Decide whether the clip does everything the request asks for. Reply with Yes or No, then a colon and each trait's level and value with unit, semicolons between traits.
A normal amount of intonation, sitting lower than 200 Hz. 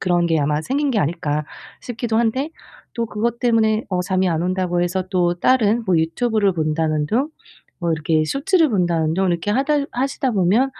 No: wide, 5.9 semitones; high, 190 Hz